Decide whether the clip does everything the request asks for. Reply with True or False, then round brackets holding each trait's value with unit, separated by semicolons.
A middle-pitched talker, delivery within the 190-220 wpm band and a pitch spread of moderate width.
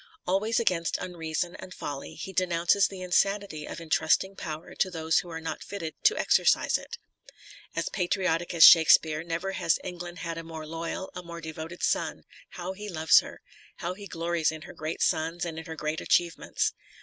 False (170 Hz; 195 wpm; 2.2 semitones)